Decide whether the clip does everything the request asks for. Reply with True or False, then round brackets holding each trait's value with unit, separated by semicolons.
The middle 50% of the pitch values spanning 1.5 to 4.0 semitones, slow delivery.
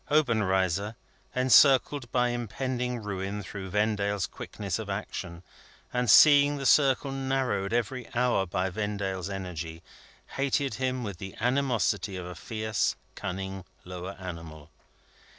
False (5.0 semitones; 120 wpm)